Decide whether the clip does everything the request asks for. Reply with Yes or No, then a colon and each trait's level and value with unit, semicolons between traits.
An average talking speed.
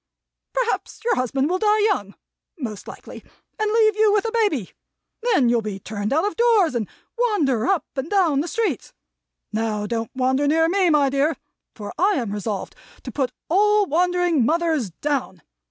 Yes: average, 170 wpm